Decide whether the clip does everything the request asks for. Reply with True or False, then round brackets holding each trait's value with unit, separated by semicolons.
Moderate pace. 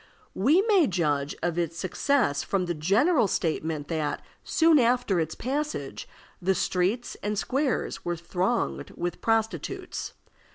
False (130 wpm)